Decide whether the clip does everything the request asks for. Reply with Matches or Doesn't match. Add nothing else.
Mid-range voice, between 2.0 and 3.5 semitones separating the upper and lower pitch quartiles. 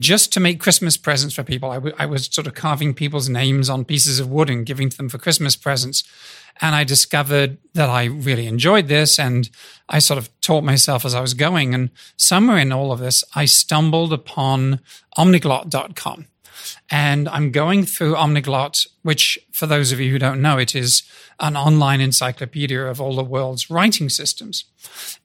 Matches